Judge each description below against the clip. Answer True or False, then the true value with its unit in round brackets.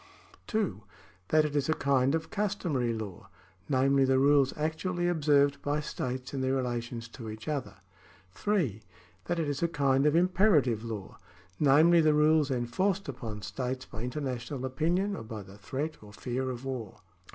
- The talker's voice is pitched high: False (135 Hz)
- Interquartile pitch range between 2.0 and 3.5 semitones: False (4.4 semitones)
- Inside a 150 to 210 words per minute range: True (165 wpm)